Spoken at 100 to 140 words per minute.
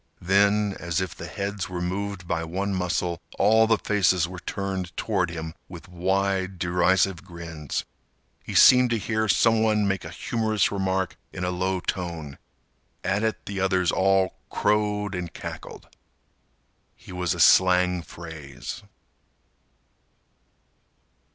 Yes: slow, 135 wpm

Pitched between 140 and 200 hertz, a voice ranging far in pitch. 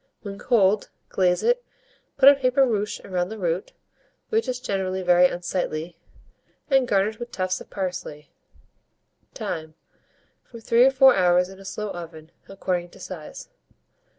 No: high, 190 Hz; average, 4.8 semitones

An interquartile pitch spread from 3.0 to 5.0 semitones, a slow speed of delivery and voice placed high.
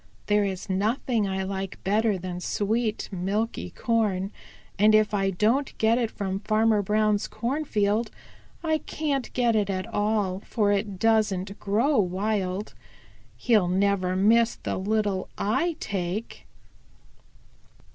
No: narrow, 2.6 semitones; slow, 125 wpm; high, 210 Hz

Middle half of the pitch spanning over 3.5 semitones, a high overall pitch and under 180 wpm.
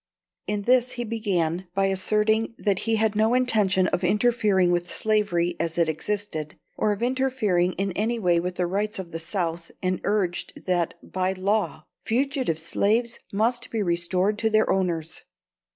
Yes: average, 3.9 semitones; high, 195 Hz; average, 165 wpm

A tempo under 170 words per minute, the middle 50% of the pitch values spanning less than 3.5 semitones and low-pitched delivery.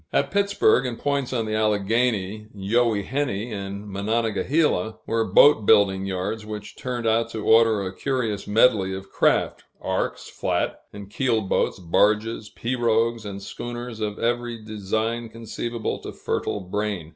Yes: average, 140 wpm; narrow, 2.6 semitones; low, 110 Hz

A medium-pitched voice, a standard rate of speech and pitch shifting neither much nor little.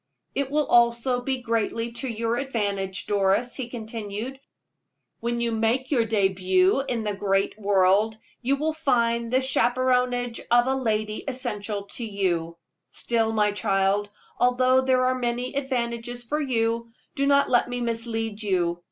No: high, 235 Hz; average, 150 wpm; average, 3.4 semitones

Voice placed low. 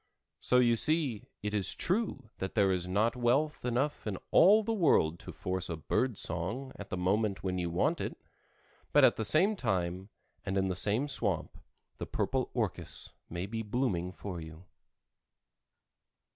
Yes: low, 105 Hz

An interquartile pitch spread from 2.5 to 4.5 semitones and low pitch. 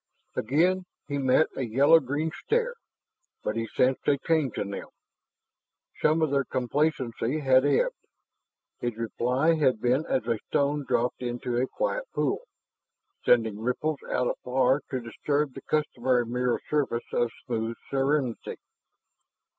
Yes: average, 3.7 semitones; low, 130 Hz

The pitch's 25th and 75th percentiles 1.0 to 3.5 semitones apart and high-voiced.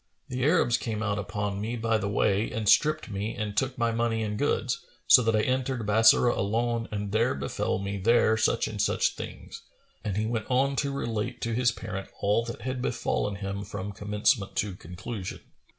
No: average, 2.8 semitones; low, 110 Hz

